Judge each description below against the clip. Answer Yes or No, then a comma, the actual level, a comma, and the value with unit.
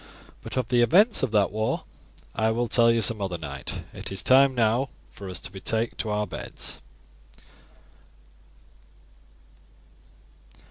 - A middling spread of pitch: Yes, average, 3.2 semitones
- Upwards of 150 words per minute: No, average, 145 wpm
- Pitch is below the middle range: Yes, low, 110 Hz